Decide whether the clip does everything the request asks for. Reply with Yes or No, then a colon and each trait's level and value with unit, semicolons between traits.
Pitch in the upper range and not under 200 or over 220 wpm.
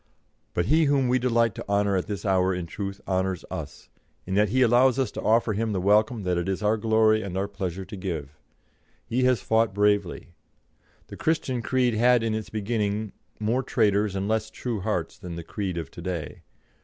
No: low, 105 Hz; fast, 205 wpm